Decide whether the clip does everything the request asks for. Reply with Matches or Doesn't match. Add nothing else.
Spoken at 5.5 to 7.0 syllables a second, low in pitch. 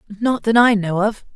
Doesn't match